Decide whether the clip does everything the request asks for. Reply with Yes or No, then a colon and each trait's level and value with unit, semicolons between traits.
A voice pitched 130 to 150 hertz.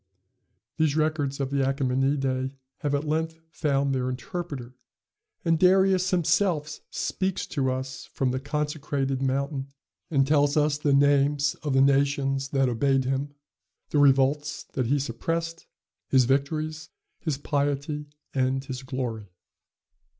Yes: medium, 140 Hz